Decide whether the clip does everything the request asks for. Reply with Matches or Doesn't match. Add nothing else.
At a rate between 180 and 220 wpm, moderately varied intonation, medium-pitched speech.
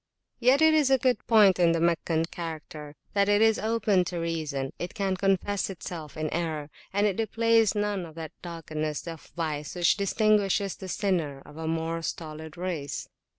Matches